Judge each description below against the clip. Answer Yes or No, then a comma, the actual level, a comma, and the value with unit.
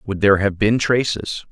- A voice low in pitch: Yes, low, 105 Hz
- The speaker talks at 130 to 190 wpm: No, average, 200 wpm